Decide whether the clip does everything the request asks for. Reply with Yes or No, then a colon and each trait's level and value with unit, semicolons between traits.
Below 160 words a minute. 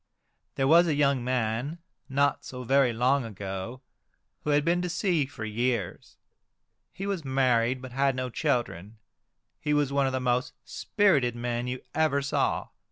No: average, 165 wpm